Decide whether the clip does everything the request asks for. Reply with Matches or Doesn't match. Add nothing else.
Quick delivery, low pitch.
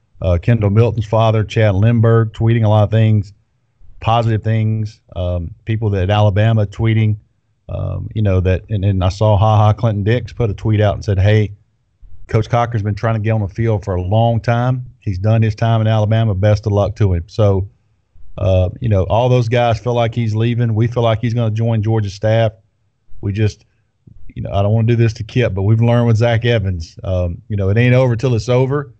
Matches